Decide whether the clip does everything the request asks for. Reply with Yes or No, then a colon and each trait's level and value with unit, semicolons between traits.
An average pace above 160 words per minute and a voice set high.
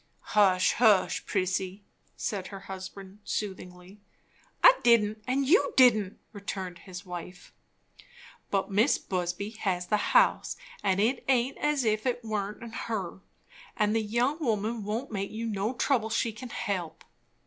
No: average, 140 wpm; high, 210 Hz